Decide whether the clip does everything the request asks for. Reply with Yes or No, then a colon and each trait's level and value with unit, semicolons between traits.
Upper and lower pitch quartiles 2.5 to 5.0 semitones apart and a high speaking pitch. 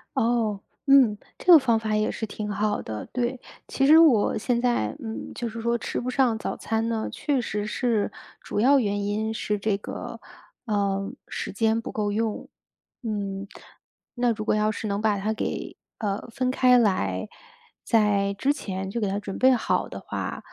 Yes: average, 2.8 semitones; high, 220 Hz